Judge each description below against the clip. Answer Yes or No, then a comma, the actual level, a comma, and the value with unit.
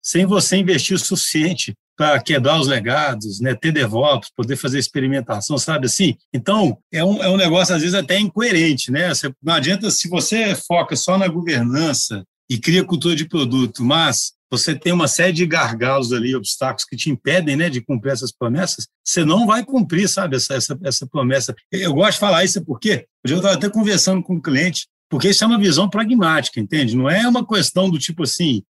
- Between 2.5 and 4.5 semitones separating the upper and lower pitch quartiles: No, wide, 5.6 semitones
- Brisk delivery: Yes, fast, 200 wpm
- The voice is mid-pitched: Yes, medium, 160 Hz